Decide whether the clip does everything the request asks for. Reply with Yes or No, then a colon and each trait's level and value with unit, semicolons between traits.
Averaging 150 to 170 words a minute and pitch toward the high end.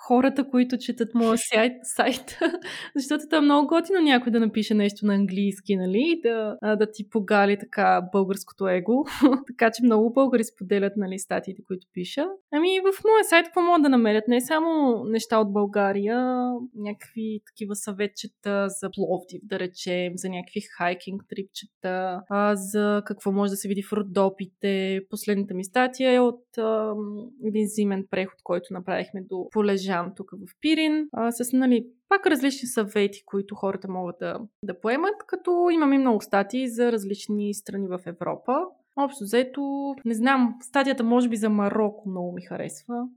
Yes: average, 160 wpm; high, 215 Hz